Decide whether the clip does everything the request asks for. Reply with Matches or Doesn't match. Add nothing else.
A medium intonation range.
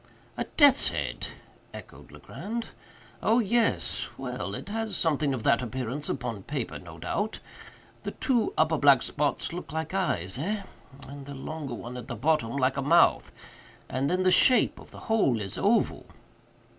Doesn't match